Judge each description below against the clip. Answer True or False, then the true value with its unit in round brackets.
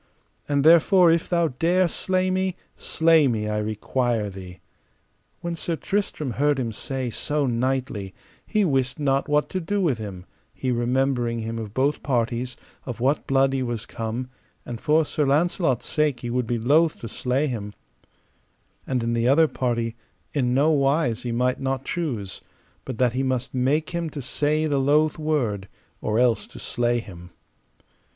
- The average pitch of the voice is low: True (130 Hz)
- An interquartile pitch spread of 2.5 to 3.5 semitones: False (4.4 semitones)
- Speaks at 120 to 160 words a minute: False (170 wpm)